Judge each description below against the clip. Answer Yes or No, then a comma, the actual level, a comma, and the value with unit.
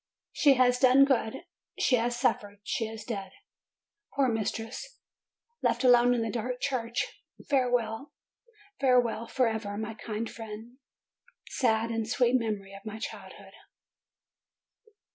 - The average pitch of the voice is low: No, high, 230 Hz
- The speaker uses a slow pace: Yes, slow, 125 wpm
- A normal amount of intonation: No, narrow, 2.3 semitones